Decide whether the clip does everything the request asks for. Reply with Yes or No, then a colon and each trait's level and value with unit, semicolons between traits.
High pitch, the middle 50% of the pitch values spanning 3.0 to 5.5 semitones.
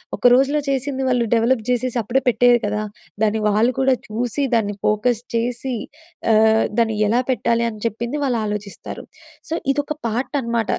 No: high, 235 Hz; narrow, 2.6 semitones